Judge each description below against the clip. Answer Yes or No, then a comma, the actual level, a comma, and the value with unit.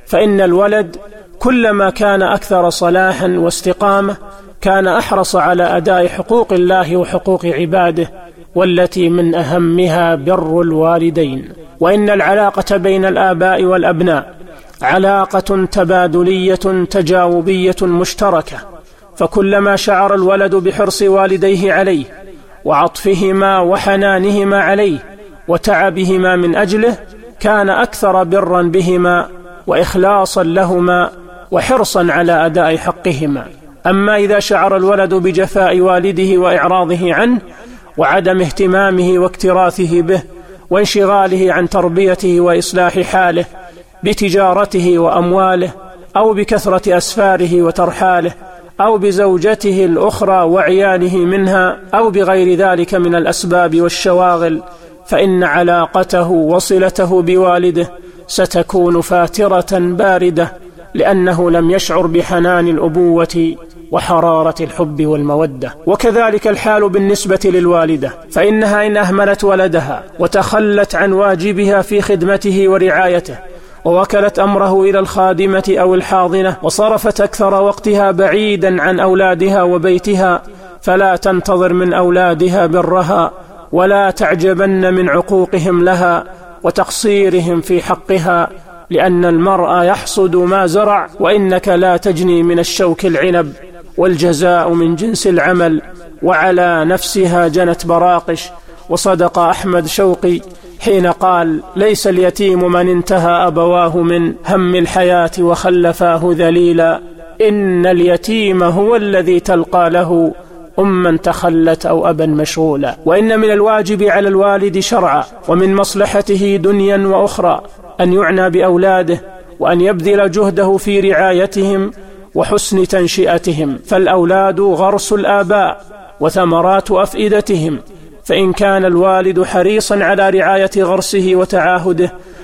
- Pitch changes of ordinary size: No, narrow, 1.8 semitones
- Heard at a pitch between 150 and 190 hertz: Yes, medium, 185 Hz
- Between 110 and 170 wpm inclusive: No, average, 100 wpm